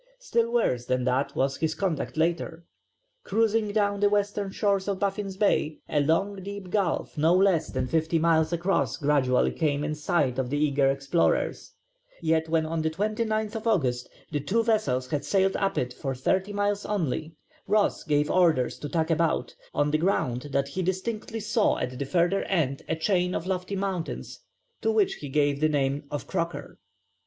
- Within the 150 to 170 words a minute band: No, average, 180 wpm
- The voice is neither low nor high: Yes, medium, 165 Hz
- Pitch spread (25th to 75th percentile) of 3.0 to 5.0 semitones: No, wide, 5.5 semitones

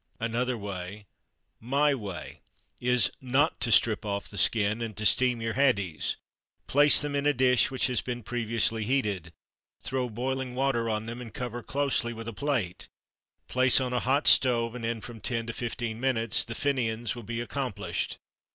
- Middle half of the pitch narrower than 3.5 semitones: Yes, narrow, 2.6 semitones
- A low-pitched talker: Yes, low, 120 Hz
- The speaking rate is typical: Yes, average, 175 wpm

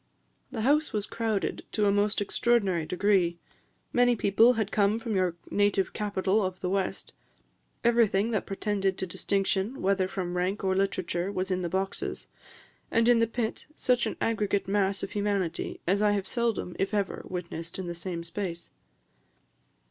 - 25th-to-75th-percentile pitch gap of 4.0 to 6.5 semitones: No, narrow, 2.4 semitones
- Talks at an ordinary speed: Yes, average, 165 wpm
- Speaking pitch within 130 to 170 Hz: No, high, 200 Hz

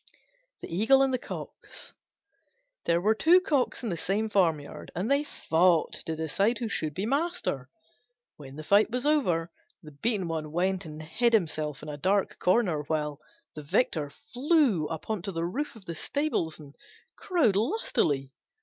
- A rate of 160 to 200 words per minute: Yes, average, 170 wpm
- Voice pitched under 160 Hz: No, medium, 185 Hz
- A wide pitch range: Yes, wide, 7.4 semitones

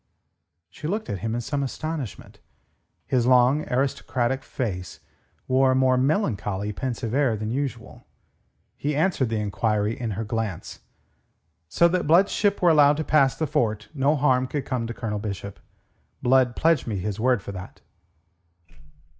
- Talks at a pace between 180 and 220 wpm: No, average, 155 wpm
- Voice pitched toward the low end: Yes, low, 125 Hz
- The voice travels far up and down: No, average, 4.7 semitones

